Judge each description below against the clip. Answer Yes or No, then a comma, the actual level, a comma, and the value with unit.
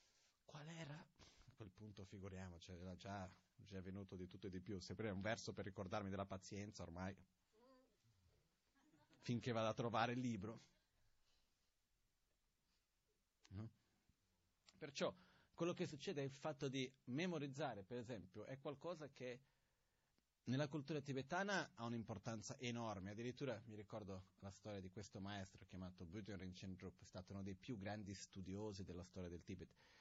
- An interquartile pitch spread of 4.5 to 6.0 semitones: Yes, average, 4.8 semitones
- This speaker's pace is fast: No, average, 145 wpm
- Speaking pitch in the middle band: No, low, 105 Hz